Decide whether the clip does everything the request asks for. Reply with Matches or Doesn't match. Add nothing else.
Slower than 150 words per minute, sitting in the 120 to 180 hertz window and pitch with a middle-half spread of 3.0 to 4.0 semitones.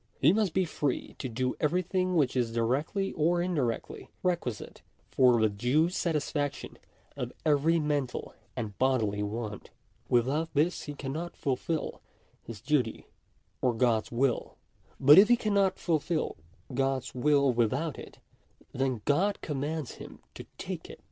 Doesn't match